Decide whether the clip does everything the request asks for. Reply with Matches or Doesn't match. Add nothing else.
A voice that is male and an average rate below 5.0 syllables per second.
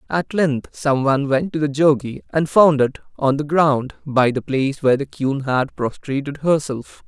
Matches